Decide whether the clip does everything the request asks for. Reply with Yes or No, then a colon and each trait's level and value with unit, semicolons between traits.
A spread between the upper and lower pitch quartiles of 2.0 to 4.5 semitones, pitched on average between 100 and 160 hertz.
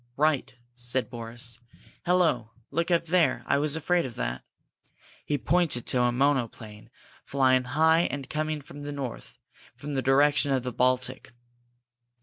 Yes: average, 3.8 semitones; low, 135 Hz